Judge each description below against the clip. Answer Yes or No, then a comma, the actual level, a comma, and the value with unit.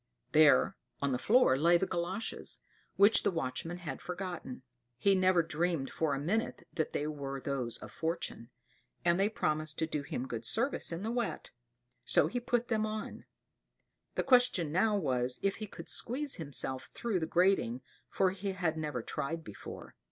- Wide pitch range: Yes, wide, 5.7 semitones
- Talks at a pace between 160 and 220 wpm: Yes, average, 175 wpm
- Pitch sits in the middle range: Yes, medium, 170 Hz